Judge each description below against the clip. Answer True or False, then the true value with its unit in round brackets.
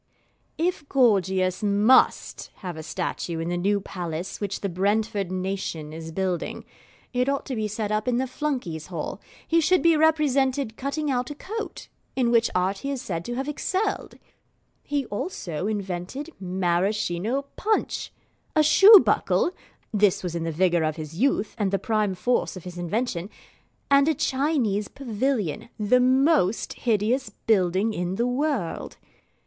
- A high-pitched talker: True (215 Hz)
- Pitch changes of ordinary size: False (6.7 semitones)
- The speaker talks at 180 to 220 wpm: False (155 wpm)